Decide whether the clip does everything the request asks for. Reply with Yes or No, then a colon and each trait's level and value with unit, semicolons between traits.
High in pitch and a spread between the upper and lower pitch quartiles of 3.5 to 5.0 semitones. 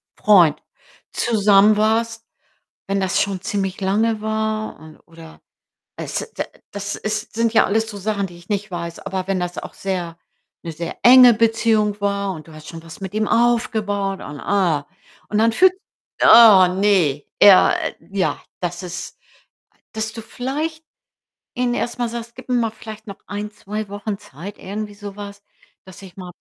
No: high, 205 Hz; average, 2.8 semitones